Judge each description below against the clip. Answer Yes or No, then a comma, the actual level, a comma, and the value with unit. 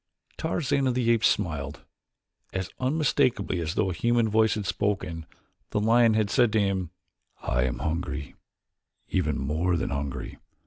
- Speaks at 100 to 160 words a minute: Yes, average, 150 wpm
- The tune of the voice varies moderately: No, wide, 6.4 semitones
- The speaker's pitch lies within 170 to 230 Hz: No, low, 100 Hz